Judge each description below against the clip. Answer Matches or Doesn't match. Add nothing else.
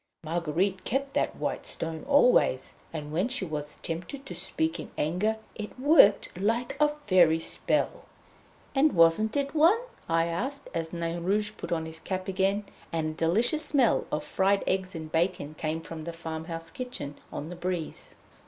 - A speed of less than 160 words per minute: Doesn't match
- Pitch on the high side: Doesn't match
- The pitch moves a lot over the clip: Matches